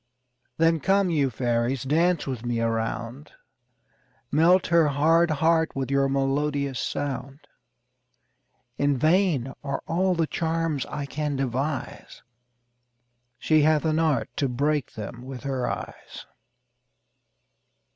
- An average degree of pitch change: Yes, average, 3.4 semitones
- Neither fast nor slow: No, slow, 120 wpm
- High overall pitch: No, medium, 145 Hz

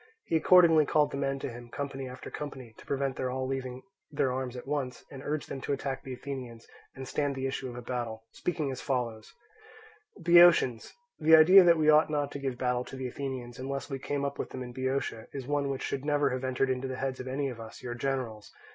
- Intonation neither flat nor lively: No, narrow, 2.1 semitones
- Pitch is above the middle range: No, low, 135 Hz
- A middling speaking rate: No, fast, 235 wpm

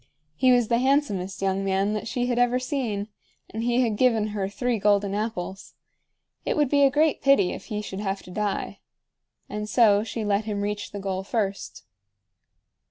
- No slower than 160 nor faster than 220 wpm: Yes, average, 185 wpm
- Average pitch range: Yes, average, 3.6 semitones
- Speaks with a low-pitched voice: No, high, 210 Hz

